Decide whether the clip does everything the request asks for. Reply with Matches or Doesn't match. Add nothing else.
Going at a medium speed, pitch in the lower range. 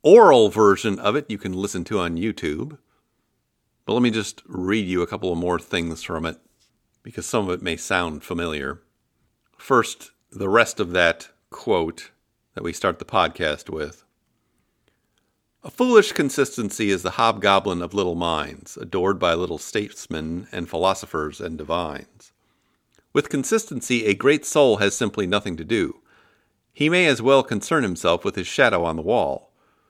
Matches